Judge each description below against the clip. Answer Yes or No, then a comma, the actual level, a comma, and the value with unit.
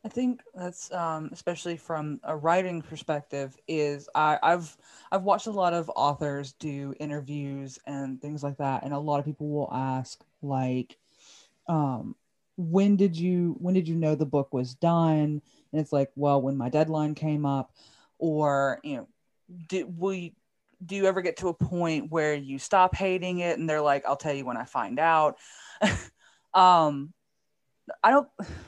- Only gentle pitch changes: No, average, 3.8 semitones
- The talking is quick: No, average, 170 wpm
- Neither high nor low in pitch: Yes, medium, 155 Hz